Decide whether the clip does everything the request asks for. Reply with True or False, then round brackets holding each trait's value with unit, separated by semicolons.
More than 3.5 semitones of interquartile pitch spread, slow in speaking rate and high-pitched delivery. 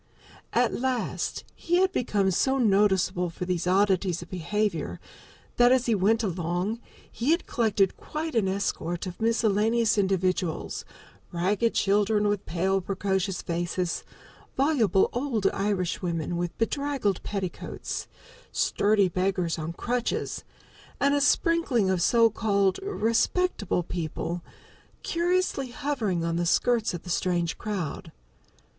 True (4.6 semitones; 125 wpm; 200 Hz)